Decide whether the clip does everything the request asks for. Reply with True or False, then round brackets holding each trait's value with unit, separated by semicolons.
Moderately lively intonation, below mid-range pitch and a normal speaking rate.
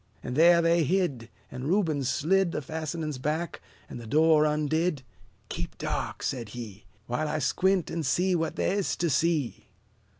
False (4.1 semitones; 155 Hz; 165 wpm)